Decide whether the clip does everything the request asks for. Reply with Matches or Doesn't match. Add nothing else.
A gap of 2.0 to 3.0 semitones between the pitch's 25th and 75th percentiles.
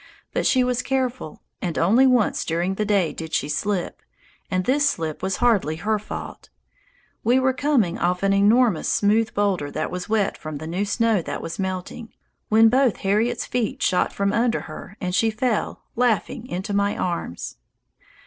Doesn't match